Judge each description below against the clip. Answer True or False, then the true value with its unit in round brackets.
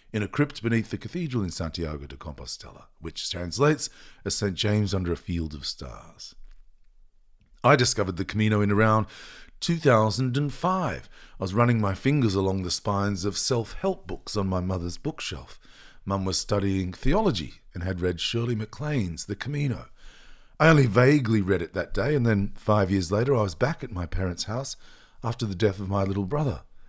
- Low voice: True (105 Hz)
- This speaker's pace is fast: False (180 wpm)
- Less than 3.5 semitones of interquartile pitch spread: False (4.7 semitones)